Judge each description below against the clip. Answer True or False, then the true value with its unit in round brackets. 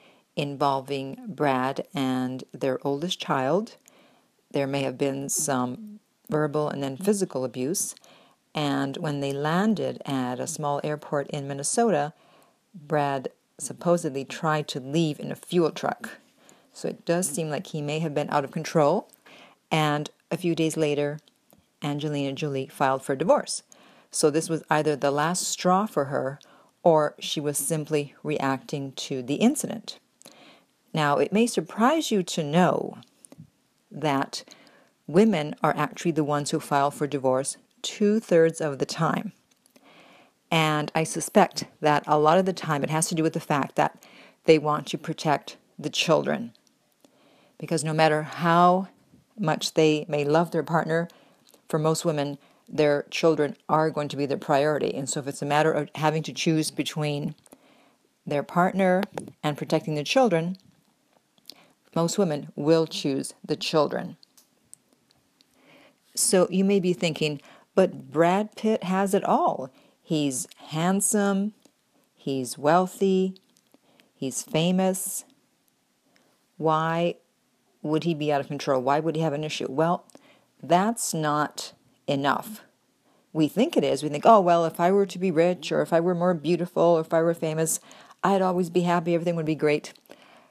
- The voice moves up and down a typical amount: True (3.7 semitones)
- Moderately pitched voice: True (160 Hz)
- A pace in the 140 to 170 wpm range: True (150 wpm)